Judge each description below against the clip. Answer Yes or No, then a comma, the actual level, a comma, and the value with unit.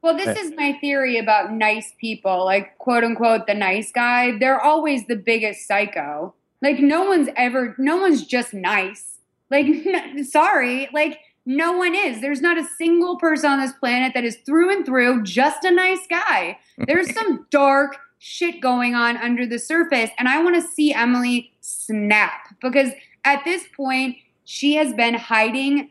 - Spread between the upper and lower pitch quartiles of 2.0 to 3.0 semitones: No, average, 4.5 semitones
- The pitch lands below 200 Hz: No, very high, 270 Hz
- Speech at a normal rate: Yes, average, 175 wpm